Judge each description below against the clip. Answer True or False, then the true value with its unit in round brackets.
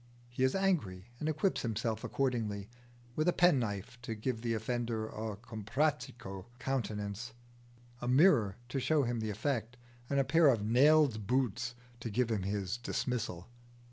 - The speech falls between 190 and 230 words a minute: False (150 wpm)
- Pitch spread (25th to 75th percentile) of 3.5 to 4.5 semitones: True (3.8 semitones)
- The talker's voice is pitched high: False (120 Hz)